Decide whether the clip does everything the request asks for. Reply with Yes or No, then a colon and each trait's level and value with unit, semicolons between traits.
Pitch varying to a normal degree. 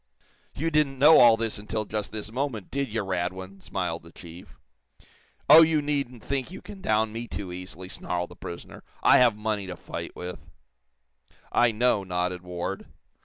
No: wide, 5.9 semitones